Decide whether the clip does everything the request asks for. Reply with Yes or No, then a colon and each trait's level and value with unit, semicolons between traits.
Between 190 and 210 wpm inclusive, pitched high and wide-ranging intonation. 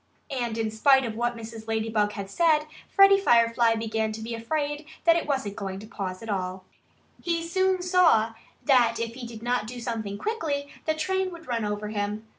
Yes: average, 195 wpm; high, 230 Hz; wide, 5.7 semitones